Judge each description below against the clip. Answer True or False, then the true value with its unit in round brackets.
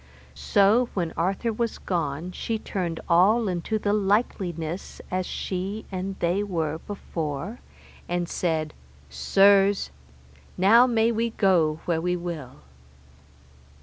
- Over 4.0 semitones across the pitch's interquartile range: False (3.6 semitones)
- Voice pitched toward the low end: False (185 Hz)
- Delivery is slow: True (115 wpm)